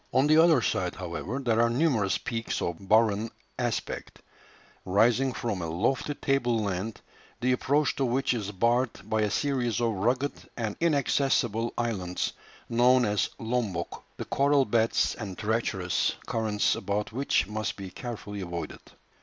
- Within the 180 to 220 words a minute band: No, average, 145 wpm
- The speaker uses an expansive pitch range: No, average, 3.8 semitones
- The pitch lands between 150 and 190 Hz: No, low, 115 Hz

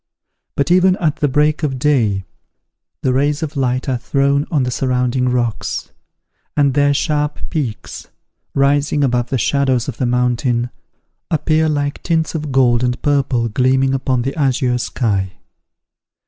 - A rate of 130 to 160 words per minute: Yes, average, 145 wpm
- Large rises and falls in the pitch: No, average, 2.9 semitones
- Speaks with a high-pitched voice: No, low, 135 Hz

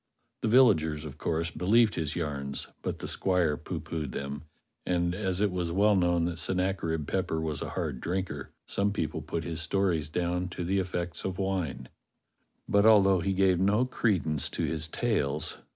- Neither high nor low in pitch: No, very low, 90 Hz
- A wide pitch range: No, average, 3.3 semitones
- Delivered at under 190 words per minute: Yes, average, 170 wpm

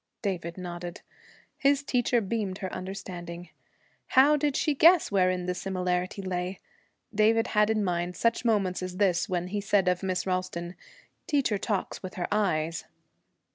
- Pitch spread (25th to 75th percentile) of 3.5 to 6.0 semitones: No, average, 3.1 semitones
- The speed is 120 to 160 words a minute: Yes, average, 150 wpm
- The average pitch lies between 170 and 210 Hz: Yes, high, 190 Hz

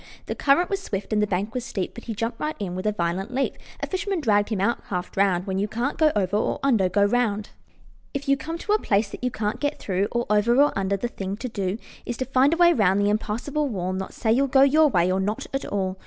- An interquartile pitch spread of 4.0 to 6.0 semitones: Yes, wide, 5.5 semitones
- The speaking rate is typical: No, fast, 270 wpm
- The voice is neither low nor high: No, high, 215 Hz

